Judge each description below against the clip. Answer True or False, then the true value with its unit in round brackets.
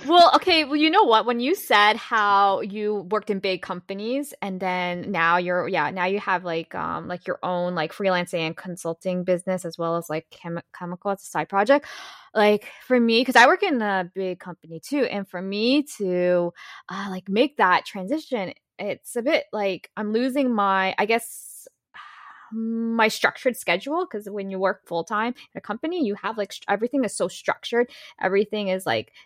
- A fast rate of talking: False (195 wpm)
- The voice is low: False (200 Hz)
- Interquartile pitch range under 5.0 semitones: False (5.3 semitones)